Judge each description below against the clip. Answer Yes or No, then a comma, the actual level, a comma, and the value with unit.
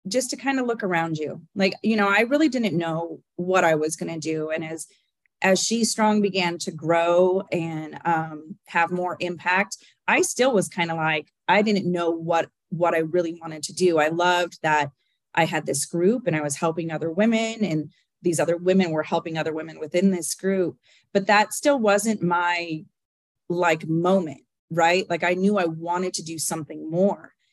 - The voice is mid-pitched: Yes, medium, 175 Hz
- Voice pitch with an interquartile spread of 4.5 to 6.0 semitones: No, average, 2.9 semitones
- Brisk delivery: No, average, 195 wpm